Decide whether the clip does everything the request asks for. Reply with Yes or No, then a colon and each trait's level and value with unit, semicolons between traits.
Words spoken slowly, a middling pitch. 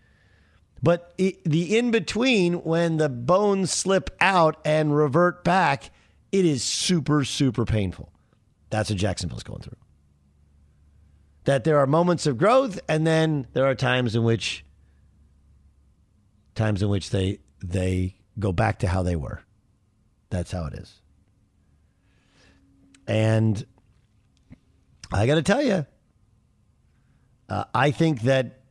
No: slow, 130 wpm; low, 110 Hz